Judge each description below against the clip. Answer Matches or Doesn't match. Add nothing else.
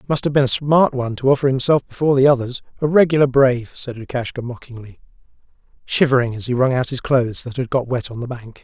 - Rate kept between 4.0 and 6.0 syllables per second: Doesn't match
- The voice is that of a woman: Doesn't match